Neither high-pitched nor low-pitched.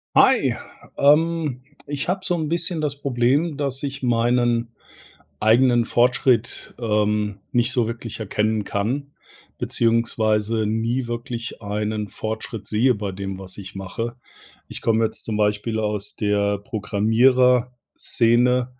No: low, 115 Hz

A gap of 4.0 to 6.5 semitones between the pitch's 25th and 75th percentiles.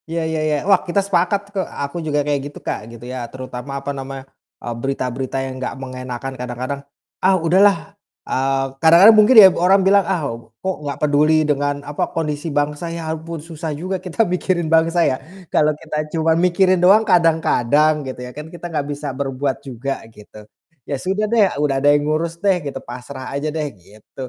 Yes: average, 4.3 semitones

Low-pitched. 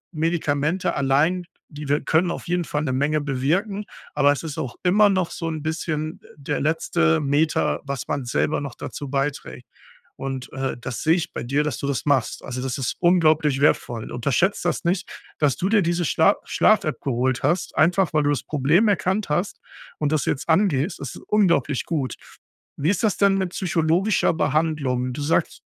No: medium, 150 Hz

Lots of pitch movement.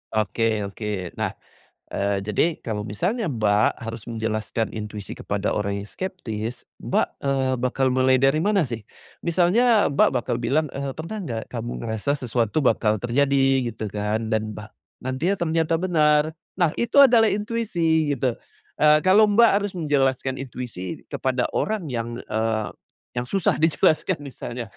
Yes: wide, 6.6 semitones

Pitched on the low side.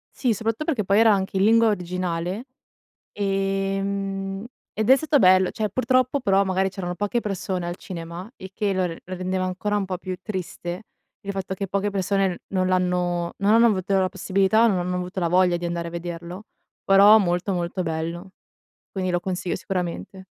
No: high, 190 Hz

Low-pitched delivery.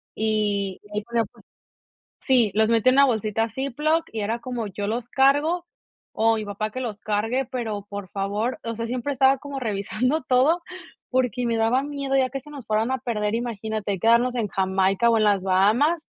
No: high, 230 Hz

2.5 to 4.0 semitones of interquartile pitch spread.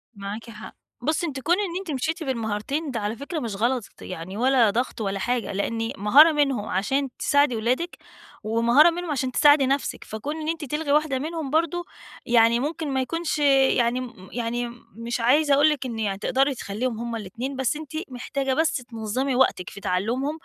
No: average, 4.4 semitones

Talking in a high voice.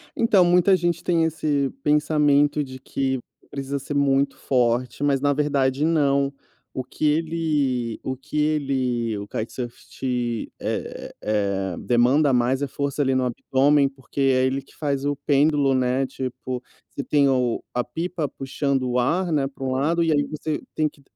No: medium, 140 Hz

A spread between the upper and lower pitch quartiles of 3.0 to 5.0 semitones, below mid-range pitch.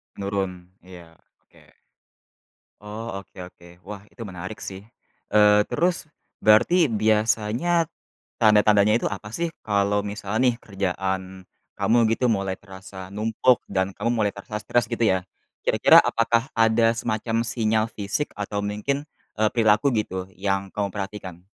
No: narrow, 2.6 semitones; low, 105 Hz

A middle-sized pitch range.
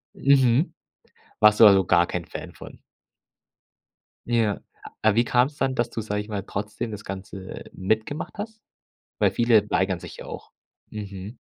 Yes: average, 3.5 semitones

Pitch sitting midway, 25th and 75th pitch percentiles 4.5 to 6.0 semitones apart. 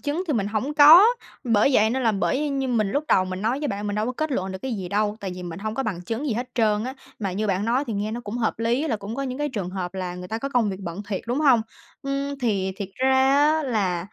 No: high, 225 Hz; average, 5.0 semitones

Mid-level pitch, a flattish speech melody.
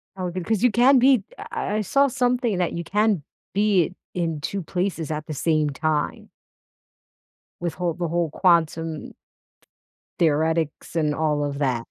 No: medium, 170 Hz; average, 4.8 semitones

